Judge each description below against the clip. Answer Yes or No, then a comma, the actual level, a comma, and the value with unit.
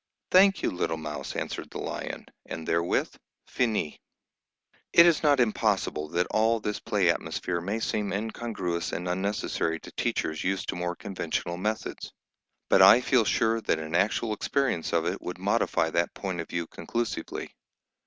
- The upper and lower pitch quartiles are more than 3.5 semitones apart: Yes, average, 4.7 semitones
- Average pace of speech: Yes, average, 160 wpm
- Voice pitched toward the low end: Yes, very low, 95 Hz